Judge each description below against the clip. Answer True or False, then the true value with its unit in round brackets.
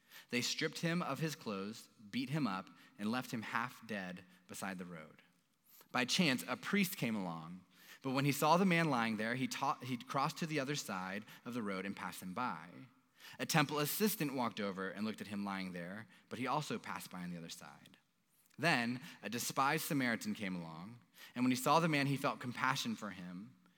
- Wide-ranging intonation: True (7.2 semitones)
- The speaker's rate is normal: False (210 wpm)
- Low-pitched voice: True (125 Hz)